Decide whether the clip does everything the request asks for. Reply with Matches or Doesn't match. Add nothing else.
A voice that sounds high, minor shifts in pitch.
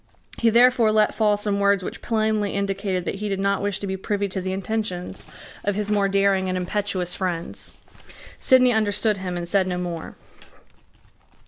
Matches